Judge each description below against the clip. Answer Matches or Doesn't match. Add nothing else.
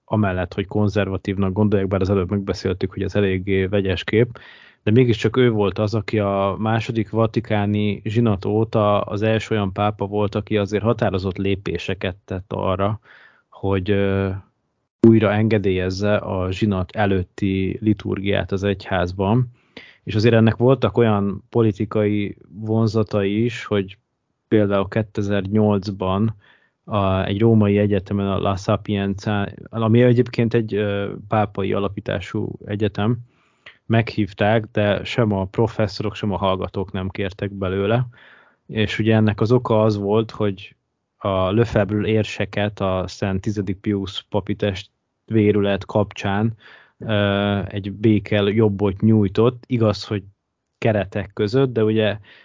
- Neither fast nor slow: Matches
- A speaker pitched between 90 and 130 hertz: Matches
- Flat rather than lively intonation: Matches